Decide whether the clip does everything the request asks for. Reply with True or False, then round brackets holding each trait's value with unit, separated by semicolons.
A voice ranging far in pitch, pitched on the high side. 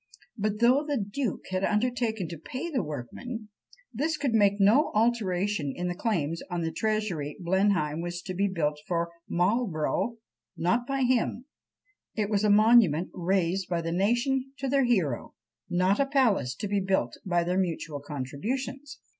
True (5.7 semitones; 200 Hz)